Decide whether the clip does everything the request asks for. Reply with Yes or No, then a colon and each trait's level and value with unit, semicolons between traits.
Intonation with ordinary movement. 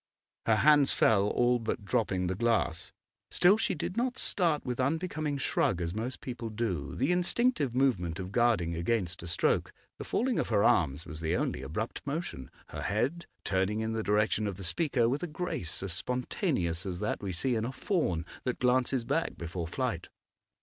No: wide, 7.1 semitones